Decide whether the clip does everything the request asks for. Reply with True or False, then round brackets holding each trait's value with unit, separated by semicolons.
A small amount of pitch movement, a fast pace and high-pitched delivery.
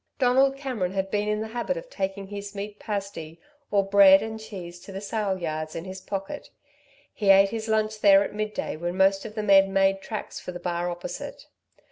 True (2.0 semitones; 210 wpm; 200 Hz)